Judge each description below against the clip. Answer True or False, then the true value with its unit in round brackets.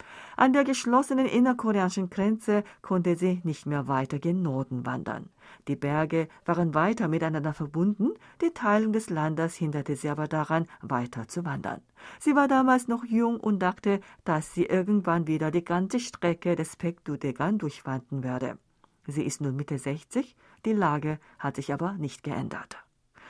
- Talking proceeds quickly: False (160 wpm)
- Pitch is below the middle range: False (170 Hz)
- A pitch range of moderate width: False (5.9 semitones)